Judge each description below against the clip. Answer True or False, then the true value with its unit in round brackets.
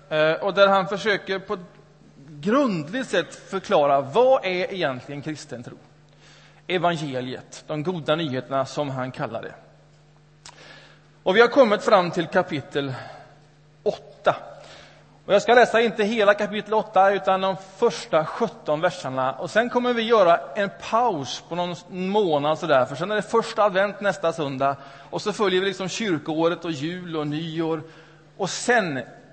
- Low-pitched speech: False (170 Hz)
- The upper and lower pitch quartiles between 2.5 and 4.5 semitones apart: False (5.2 semitones)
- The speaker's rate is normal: True (150 wpm)